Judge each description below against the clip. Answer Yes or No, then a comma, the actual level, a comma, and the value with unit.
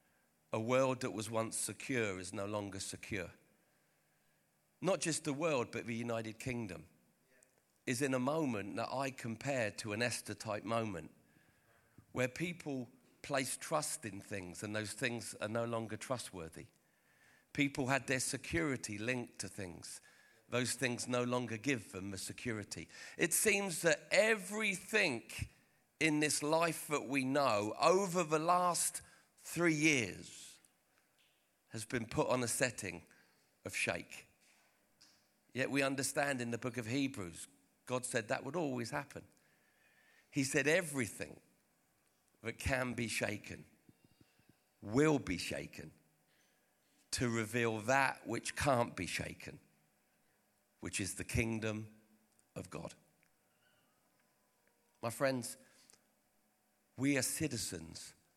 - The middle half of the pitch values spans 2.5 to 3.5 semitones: No, average, 4.7 semitones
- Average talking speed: No, slow, 125 wpm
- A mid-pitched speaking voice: No, low, 120 Hz